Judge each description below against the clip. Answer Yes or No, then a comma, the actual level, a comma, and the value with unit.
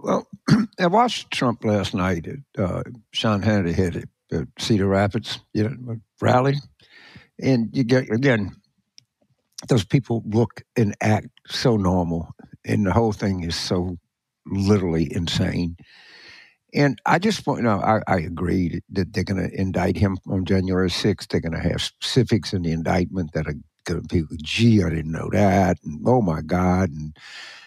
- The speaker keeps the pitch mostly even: No, average, 4.5 semitones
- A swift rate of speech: No, average, 165 wpm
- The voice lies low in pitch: Yes, low, 100 Hz